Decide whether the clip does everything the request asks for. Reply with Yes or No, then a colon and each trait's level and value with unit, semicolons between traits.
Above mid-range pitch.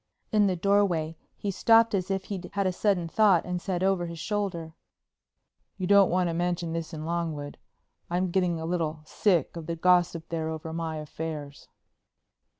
No: medium, 175 Hz